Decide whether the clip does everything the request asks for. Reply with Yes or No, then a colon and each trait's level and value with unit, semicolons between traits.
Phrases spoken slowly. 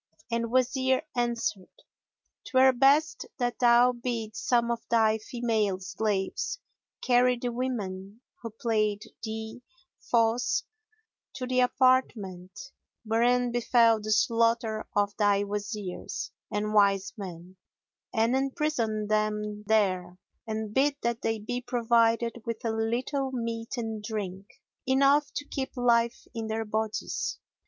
Yes: slow, 125 wpm